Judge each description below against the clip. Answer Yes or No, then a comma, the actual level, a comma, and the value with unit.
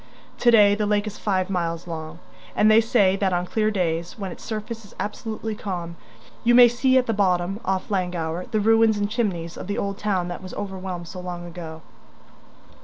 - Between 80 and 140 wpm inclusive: No, average, 200 wpm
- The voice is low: No, high, 195 Hz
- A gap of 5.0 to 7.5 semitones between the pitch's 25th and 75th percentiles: No, average, 3.4 semitones